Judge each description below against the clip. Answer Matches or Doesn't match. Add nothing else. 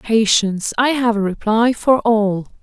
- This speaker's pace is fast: Doesn't match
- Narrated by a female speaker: Matches